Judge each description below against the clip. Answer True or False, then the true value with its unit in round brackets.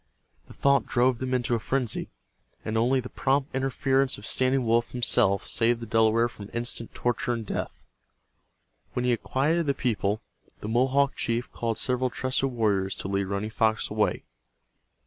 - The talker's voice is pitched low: True (120 Hz)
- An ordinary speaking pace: True (165 wpm)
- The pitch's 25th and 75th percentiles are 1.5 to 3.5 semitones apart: True (2.6 semitones)